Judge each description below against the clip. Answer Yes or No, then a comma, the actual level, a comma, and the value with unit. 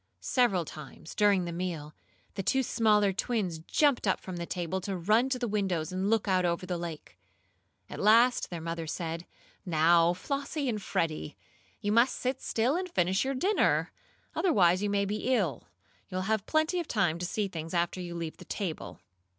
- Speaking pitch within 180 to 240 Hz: Yes, high, 190 Hz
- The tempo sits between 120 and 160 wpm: No, average, 185 wpm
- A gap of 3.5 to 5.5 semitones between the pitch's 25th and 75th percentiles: Yes, average, 5.1 semitones